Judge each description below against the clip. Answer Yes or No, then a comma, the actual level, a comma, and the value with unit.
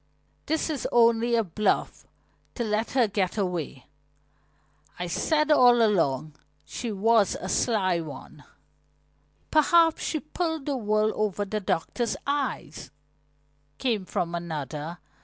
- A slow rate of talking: Yes, slow, 120 wpm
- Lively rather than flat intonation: Yes, wide, 5.9 semitones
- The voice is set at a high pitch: Yes, high, 215 Hz